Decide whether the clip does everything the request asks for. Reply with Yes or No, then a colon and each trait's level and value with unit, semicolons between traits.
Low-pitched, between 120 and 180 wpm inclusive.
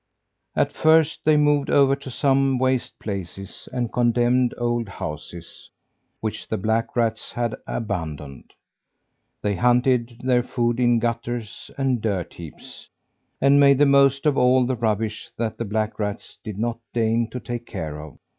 Yes: low, 120 Hz; average, 155 wpm